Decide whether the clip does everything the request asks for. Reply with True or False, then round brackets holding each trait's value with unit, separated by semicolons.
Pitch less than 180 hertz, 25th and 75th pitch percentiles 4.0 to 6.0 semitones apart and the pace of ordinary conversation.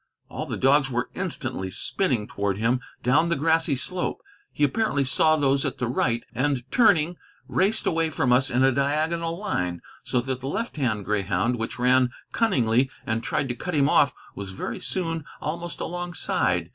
True (135 Hz; 5.1 semitones; 175 wpm)